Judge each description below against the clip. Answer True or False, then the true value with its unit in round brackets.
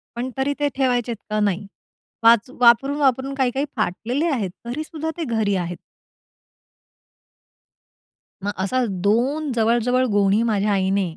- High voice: True (235 Hz)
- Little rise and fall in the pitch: False (4.5 semitones)